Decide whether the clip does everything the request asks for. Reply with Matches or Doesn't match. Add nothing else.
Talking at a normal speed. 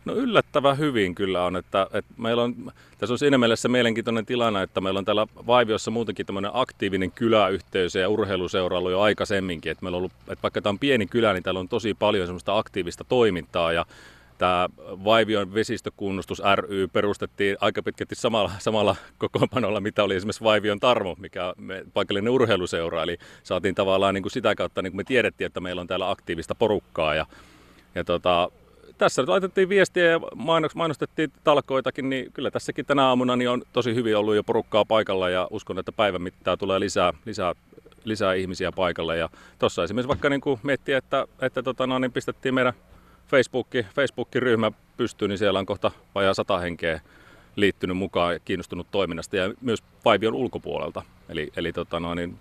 Doesn't match